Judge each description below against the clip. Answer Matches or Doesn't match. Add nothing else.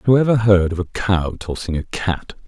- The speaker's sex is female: Doesn't match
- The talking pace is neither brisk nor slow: Doesn't match